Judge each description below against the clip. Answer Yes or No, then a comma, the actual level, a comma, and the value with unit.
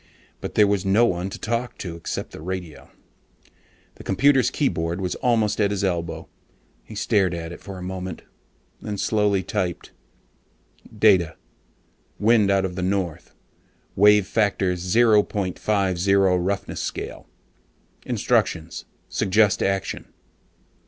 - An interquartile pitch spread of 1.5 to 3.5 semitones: Yes, narrow, 2.5 semitones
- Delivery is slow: Yes, slow, 125 wpm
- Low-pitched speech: Yes, very low, 95 Hz